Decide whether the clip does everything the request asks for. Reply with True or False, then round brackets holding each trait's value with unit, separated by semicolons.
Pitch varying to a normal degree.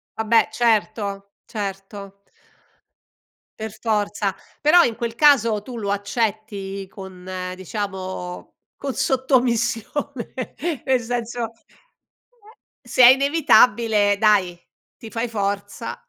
True (3.3 semitones)